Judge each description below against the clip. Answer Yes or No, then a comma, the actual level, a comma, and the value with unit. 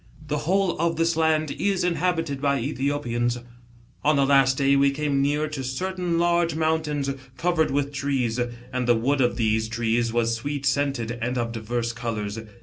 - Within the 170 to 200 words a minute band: Yes, average, 175 wpm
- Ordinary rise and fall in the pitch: Yes, average, 4.6 semitones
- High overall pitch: No, medium, 140 Hz